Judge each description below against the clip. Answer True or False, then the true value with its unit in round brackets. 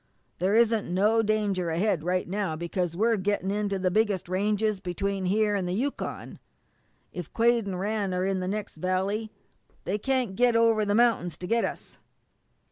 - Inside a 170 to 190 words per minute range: True (180 wpm)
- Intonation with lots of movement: False (2.9 semitones)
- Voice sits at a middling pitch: False (200 Hz)